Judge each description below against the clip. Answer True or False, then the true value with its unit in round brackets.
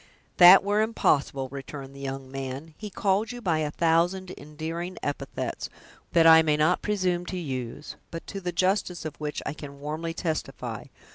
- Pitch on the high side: False (160 Hz)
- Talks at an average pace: True (170 wpm)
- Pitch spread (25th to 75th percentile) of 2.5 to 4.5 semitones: True (4.2 semitones)